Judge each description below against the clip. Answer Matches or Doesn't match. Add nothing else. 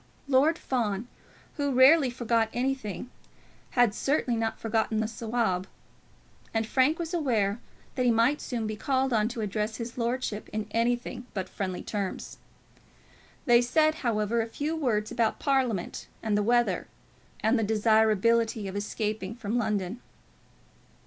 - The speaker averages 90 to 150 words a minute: Matches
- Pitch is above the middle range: Matches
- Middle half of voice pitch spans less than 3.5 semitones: Matches